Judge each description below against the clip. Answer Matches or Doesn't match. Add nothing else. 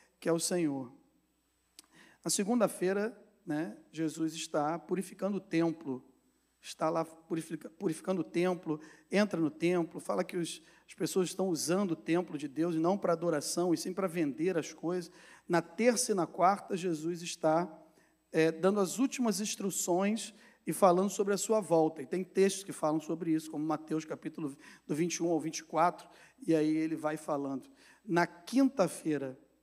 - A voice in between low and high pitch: Matches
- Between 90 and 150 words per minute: Doesn't match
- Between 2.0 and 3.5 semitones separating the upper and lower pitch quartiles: Matches